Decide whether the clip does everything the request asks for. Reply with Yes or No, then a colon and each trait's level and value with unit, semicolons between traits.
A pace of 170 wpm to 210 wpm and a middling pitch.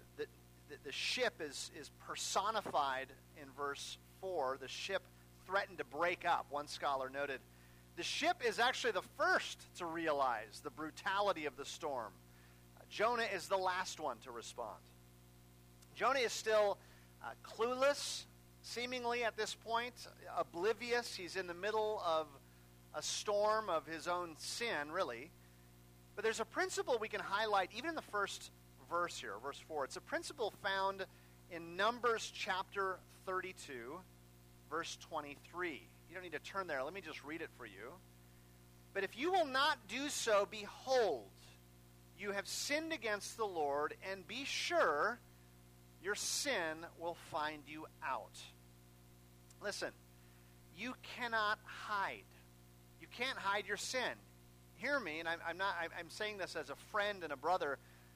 No: average, 150 wpm; medium, 155 Hz